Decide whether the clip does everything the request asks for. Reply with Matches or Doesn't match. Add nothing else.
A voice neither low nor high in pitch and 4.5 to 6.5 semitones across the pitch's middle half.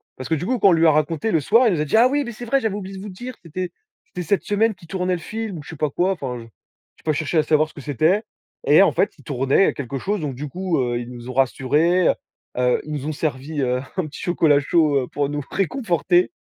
Matches